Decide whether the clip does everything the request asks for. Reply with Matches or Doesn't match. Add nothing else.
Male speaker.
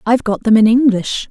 Doesn't match